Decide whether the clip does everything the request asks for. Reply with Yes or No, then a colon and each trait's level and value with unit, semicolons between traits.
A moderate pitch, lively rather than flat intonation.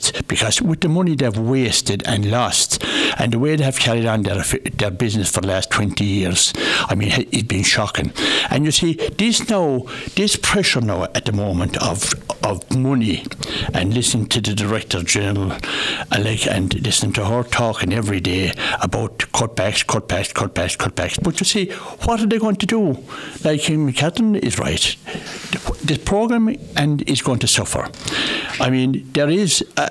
No: low, 125 Hz; wide, 6.9 semitones